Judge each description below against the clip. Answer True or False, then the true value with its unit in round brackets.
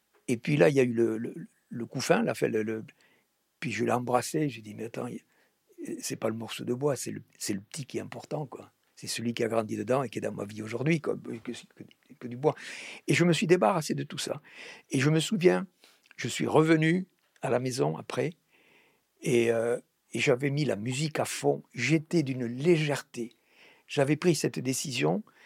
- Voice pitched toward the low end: True (130 Hz)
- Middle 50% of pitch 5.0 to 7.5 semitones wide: True (5.4 semitones)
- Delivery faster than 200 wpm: True (215 wpm)